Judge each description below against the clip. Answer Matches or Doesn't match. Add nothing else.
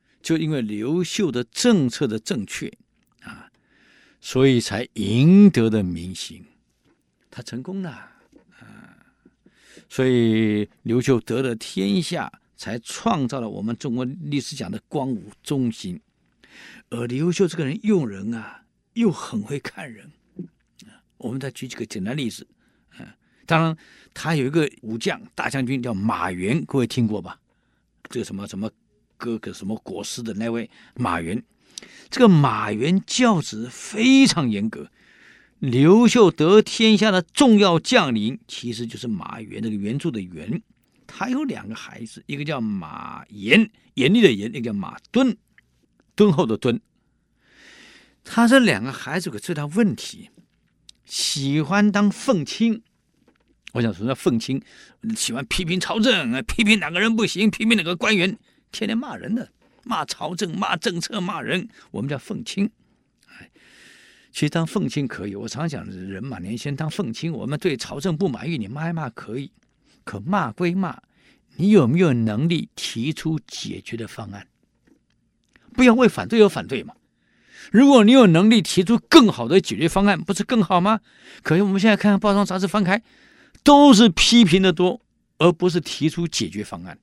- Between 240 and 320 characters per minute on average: Doesn't match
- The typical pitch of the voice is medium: Matches